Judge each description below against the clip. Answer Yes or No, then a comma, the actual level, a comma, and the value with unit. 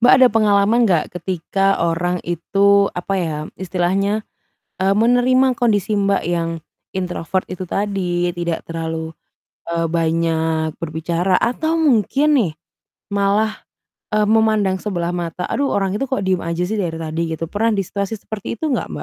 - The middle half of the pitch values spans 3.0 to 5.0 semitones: Yes, average, 4.0 semitones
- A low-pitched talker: No, high, 190 Hz